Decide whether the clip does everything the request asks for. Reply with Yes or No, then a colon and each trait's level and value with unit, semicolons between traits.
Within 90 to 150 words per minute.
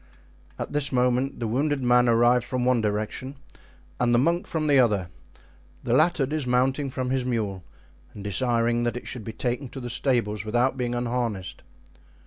No: average, 170 wpm